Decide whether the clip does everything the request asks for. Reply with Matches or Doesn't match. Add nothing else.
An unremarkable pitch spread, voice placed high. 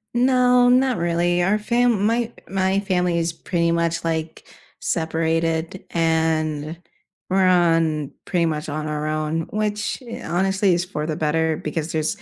Doesn't match